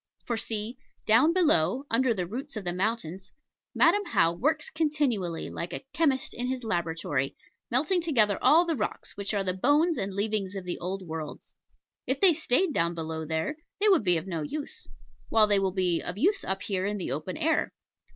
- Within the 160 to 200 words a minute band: Yes, average, 195 wpm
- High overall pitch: Yes, high, 210 Hz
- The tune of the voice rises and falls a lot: Yes, wide, 8.2 semitones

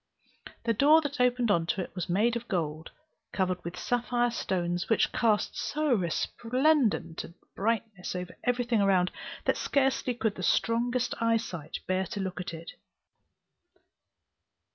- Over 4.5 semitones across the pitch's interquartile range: Yes, average, 5.1 semitones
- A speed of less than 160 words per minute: Yes, average, 140 wpm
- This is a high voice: Yes, high, 220 Hz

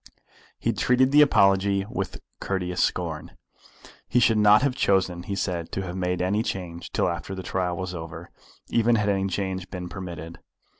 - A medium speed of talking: Yes, average, 170 wpm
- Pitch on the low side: Yes, very low, 95 Hz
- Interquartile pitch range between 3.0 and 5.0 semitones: No, narrow, 2.5 semitones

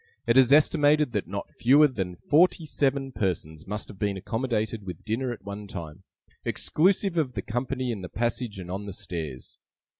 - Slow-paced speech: No, average, 180 wpm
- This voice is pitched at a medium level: No, low, 115 Hz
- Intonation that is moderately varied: No, wide, 5.7 semitones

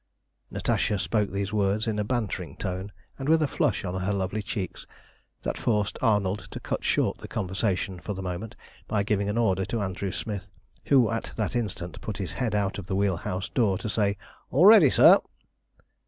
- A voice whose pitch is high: No, low, 100 Hz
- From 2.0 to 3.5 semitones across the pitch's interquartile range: Yes, average, 2.7 semitones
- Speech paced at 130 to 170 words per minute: No, average, 195 wpm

